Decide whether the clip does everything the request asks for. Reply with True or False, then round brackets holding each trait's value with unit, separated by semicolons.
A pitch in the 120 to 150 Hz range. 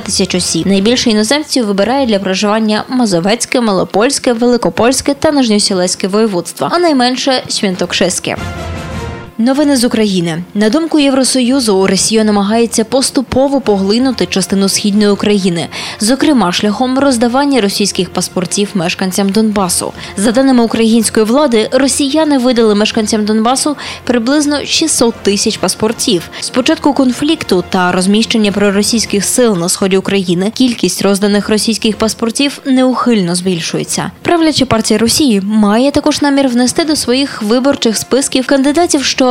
False (225 Hz)